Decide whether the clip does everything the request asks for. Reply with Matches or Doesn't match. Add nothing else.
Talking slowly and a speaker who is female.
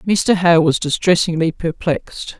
Matches